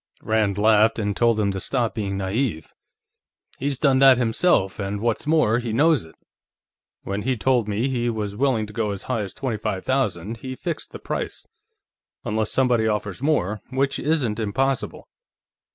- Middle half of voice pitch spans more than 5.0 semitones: No, average, 4.2 semitones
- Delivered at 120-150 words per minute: No, average, 170 wpm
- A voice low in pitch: Yes, low, 110 Hz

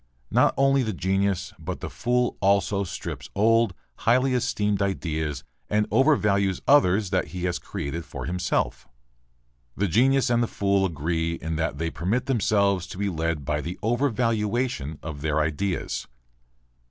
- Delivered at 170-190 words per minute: No, average, 150 wpm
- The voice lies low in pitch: Yes, very low, 95 Hz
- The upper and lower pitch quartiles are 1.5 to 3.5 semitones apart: No, wide, 5.6 semitones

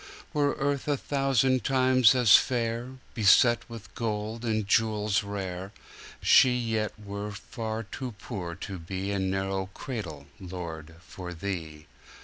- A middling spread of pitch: Yes, average, 4.2 semitones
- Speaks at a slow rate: Yes, slow, 120 wpm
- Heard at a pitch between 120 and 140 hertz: No, low, 105 Hz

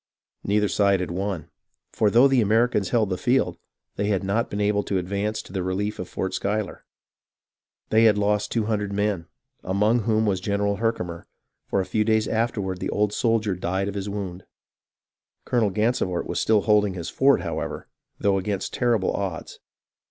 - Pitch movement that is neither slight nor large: No, narrow, 2.2 semitones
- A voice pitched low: Yes, low, 105 Hz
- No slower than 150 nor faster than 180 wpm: Yes, average, 175 wpm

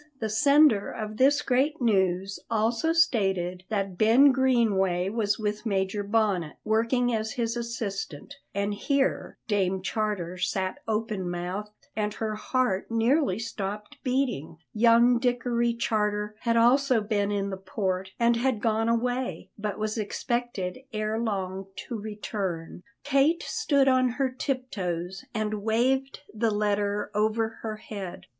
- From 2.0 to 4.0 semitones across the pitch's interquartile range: Yes, average, 3.3 semitones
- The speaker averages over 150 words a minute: No, slow, 135 wpm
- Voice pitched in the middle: No, high, 215 Hz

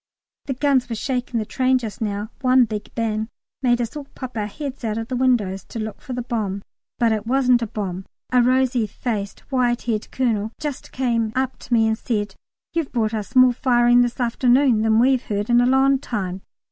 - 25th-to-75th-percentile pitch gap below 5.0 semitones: Yes, average, 2.9 semitones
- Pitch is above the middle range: Yes, high, 240 Hz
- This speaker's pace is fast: Yes, fast, 210 wpm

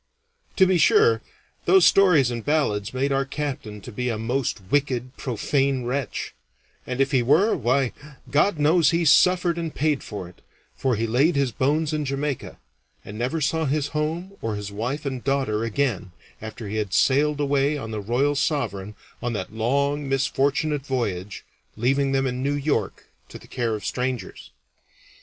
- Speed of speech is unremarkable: Yes, average, 170 wpm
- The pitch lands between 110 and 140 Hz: Yes, low, 135 Hz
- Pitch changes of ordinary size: Yes, average, 4.0 semitones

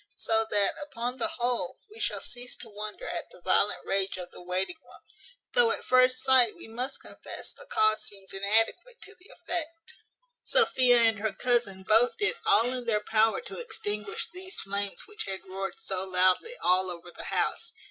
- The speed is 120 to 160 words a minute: No, average, 185 wpm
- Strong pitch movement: Yes, wide, 7.4 semitones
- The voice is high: Yes, high, 225 Hz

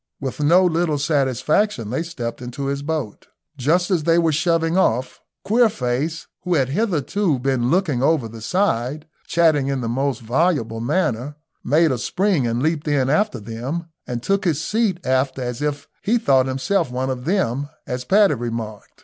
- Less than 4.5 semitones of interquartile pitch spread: No, average, 5.3 semitones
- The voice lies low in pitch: No, medium, 145 Hz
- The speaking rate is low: No, average, 170 wpm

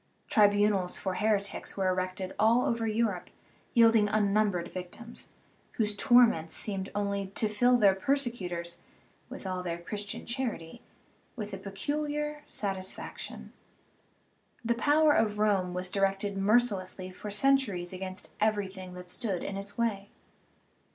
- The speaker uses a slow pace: Yes, slow, 125 wpm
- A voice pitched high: Yes, high, 205 Hz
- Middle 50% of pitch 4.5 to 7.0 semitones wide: No, average, 3.4 semitones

